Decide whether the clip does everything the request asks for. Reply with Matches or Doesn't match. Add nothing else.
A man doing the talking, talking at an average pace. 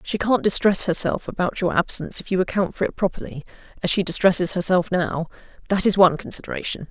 Doesn't match